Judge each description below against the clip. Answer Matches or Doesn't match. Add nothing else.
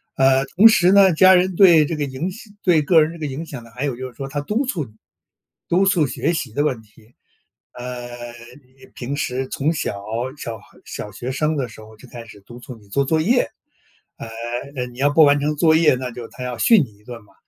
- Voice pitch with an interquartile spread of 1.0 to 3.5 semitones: Doesn't match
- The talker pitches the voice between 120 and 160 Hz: Matches